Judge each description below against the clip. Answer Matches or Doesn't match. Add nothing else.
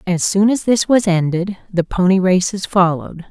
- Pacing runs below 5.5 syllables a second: Matches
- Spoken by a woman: Matches